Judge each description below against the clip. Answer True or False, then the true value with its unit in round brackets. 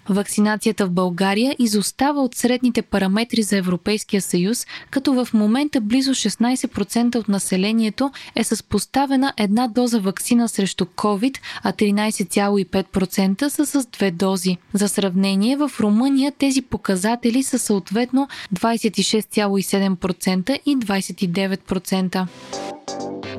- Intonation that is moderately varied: True (4.1 semitones)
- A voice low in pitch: False (215 Hz)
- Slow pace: True (110 wpm)